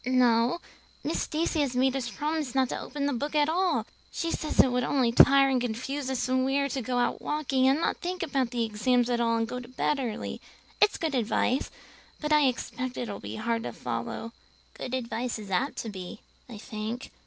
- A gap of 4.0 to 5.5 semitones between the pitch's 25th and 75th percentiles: No, average, 3.2 semitones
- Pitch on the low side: No, very high, 255 Hz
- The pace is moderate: No, fast, 220 wpm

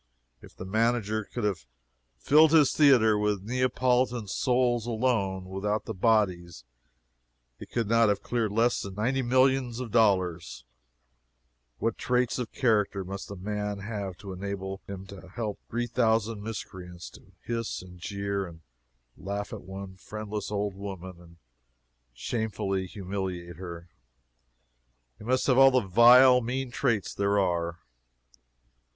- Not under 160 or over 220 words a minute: No, average, 140 wpm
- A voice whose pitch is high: No, low, 105 Hz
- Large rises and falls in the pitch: No, average, 3.9 semitones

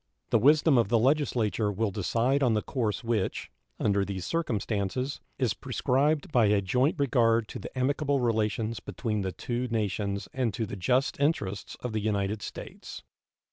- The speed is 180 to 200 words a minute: No, average, 165 wpm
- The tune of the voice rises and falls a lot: No, average, 4.0 semitones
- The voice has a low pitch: Yes, low, 115 Hz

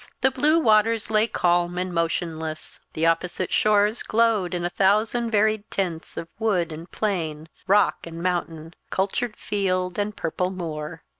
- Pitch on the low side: No, medium, 185 Hz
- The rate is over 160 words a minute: No, average, 150 wpm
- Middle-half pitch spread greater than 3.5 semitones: Yes, average, 4.1 semitones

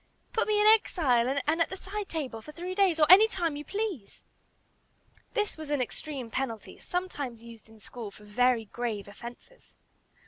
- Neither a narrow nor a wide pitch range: No, wide, 7.9 semitones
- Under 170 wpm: No, average, 175 wpm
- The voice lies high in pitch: Yes, very high, 290 Hz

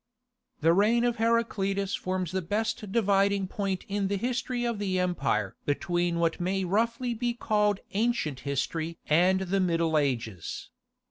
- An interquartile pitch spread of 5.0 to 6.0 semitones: No, average, 4.3 semitones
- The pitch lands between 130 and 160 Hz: No, high, 195 Hz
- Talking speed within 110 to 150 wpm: Yes, average, 145 wpm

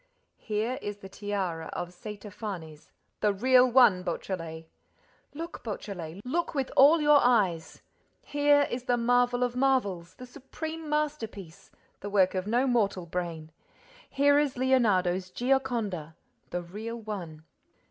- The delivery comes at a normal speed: No, slow, 130 wpm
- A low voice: No, high, 215 Hz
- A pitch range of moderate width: No, wide, 6.0 semitones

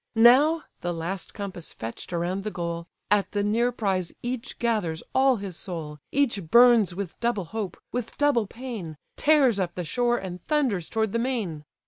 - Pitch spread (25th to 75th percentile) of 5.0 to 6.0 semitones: Yes, wide, 5.5 semitones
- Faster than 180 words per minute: No, average, 170 wpm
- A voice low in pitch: No, high, 205 Hz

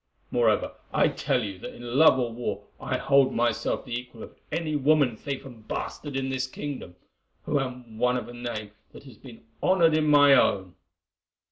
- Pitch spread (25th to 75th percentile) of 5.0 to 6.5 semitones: No, average, 3.2 semitones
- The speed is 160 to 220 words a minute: Yes, average, 190 wpm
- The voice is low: Yes, low, 130 Hz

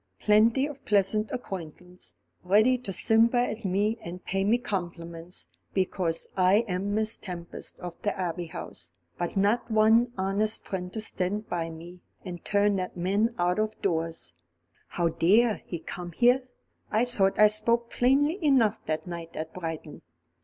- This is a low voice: No, high, 195 Hz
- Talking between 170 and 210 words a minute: No, average, 155 wpm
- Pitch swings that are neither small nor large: Yes, average, 3.9 semitones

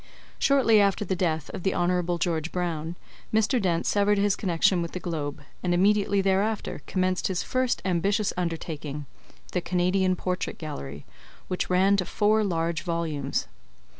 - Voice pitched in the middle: Yes, medium, 180 Hz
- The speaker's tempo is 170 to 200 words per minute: No, average, 150 wpm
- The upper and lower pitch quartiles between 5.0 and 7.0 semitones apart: No, average, 3.1 semitones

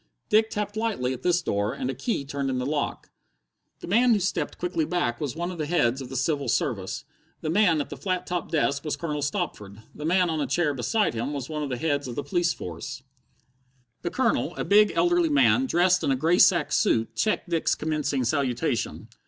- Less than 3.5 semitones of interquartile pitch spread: No, average, 5.0 semitones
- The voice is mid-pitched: Yes, medium, 155 Hz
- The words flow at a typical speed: No, fast, 220 wpm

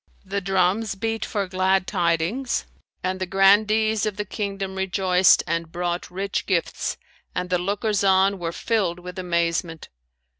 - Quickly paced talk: No, average, 145 wpm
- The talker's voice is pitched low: No, high, 190 Hz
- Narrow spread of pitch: Yes, narrow, 2.1 semitones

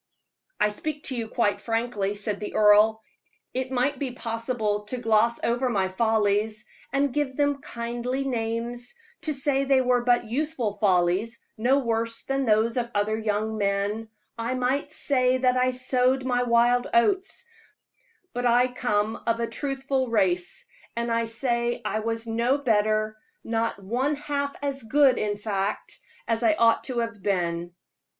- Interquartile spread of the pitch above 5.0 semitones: No, average, 3.0 semitones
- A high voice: Yes, high, 235 Hz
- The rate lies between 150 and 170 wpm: Yes, average, 155 wpm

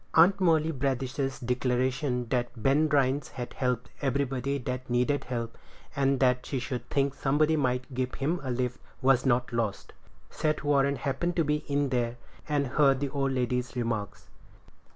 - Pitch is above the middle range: No, low, 130 Hz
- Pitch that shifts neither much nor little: No, narrow, 2.2 semitones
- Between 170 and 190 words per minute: No, average, 160 wpm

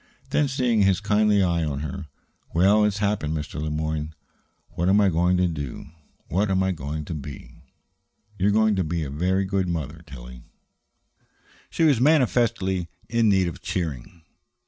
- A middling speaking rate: Yes, average, 170 wpm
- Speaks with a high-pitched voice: No, very low, 90 Hz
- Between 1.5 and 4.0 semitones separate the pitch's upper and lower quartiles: No, average, 5.0 semitones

